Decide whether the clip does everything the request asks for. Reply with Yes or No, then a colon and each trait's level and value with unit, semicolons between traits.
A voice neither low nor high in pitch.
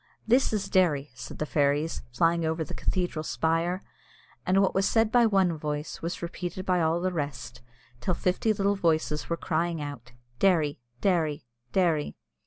Yes: medium, 170 Hz